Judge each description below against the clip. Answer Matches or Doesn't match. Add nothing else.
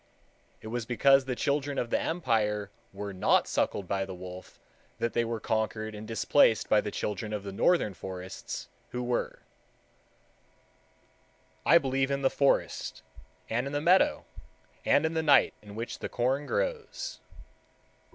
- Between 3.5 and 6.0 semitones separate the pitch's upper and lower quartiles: Matches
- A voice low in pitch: Matches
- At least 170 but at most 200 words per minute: Doesn't match